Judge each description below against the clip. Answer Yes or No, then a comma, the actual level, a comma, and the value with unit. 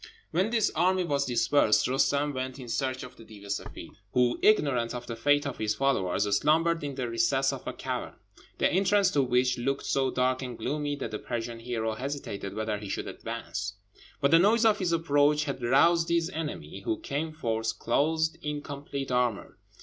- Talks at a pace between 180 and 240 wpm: Yes, average, 195 wpm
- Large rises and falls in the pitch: No, average, 4.4 semitones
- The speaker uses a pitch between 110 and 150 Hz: Yes, low, 135 Hz